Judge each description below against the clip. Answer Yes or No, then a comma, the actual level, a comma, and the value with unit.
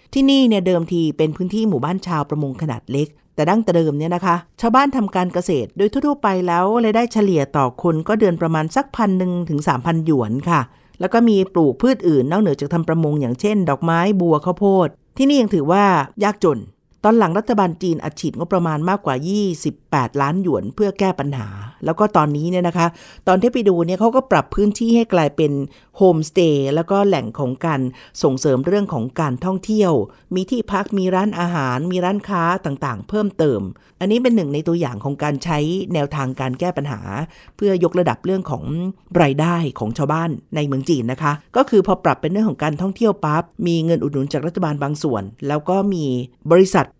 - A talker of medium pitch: Yes, medium, 170 Hz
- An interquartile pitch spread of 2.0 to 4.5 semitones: No, average, 4.9 semitones